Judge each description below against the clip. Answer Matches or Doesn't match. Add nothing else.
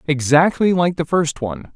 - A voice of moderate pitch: Matches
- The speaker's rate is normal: Matches